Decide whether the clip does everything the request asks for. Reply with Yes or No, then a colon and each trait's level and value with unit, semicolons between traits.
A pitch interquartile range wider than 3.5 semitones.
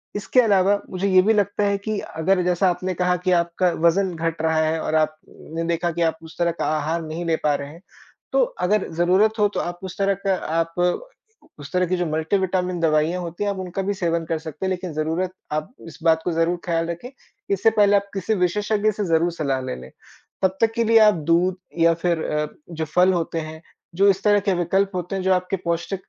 No: average, 3.0 semitones